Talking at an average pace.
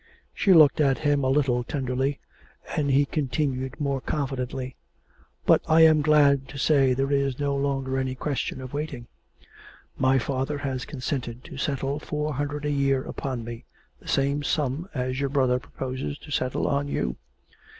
Yes: average, 160 wpm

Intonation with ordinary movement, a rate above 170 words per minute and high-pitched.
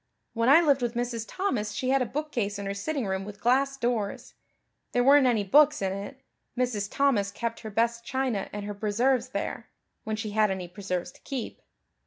Yes: average, 4.4 semitones; average, 200 wpm; high, 230 Hz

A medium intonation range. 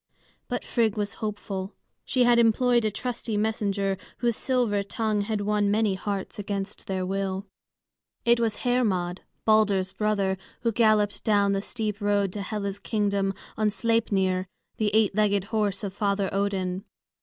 No: narrow, 2.0 semitones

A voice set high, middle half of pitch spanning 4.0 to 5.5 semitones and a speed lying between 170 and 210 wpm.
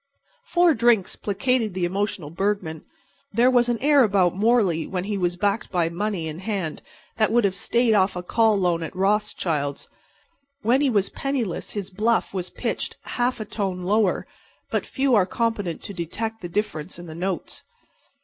Yes: high, 200 Hz; average, 4.3 semitones; average, 175 wpm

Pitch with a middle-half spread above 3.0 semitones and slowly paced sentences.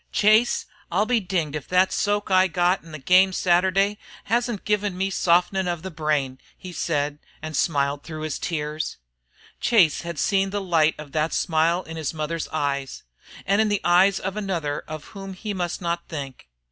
No: average, 3.9 semitones; average, 185 wpm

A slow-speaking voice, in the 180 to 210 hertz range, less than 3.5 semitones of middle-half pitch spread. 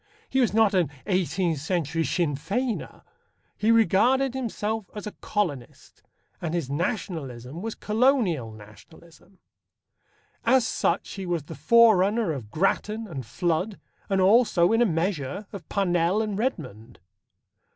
No: slow, 130 wpm; medium, 185 Hz; wide, 5.5 semitones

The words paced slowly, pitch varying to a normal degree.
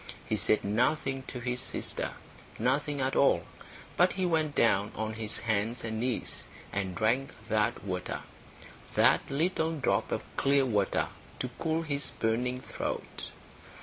No: average, 145 wpm; average, 4.4 semitones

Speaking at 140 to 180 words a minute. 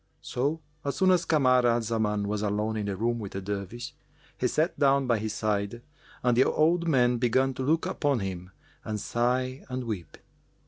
No: average, 190 wpm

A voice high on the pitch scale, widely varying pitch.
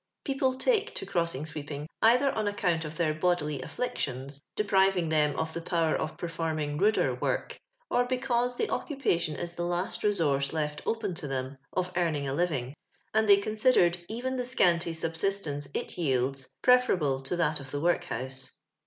No: medium, 170 Hz; wide, 6.1 semitones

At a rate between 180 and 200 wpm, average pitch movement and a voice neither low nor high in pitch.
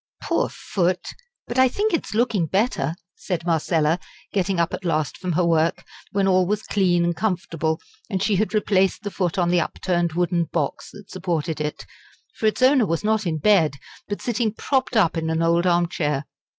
Yes: average, 190 wpm; average, 3.8 semitones; medium, 180 Hz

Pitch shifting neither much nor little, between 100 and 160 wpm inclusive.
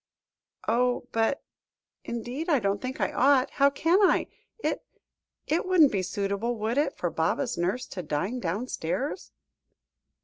No: wide, 5.8 semitones; average, 140 wpm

